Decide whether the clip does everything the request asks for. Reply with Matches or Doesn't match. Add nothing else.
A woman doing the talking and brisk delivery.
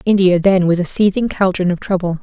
Matches